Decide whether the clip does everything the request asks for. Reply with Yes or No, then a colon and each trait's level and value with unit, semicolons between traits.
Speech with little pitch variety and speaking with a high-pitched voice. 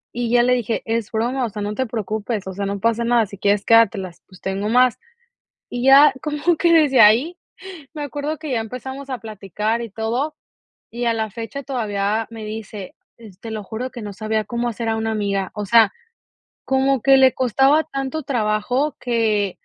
No: average, 3.7 semitones; high, 230 Hz